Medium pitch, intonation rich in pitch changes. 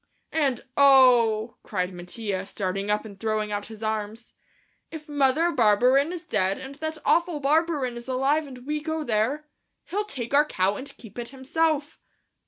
No: very high, 255 Hz; wide, 5.8 semitones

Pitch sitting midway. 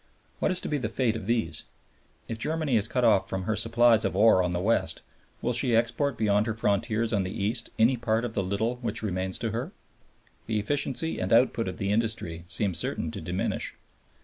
No: low, 110 Hz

